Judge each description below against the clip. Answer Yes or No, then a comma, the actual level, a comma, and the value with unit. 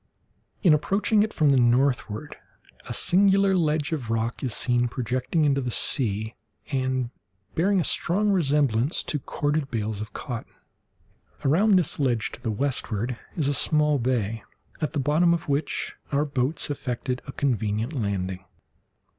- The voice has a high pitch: No, low, 135 Hz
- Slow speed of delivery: No, average, 150 wpm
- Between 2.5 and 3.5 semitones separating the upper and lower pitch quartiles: No, average, 4.4 semitones